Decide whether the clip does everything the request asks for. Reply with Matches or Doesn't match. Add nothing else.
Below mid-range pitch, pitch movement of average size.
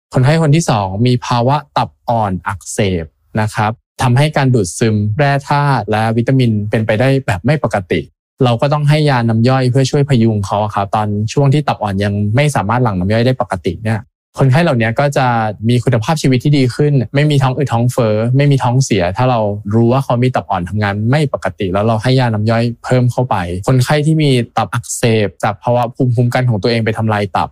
Matches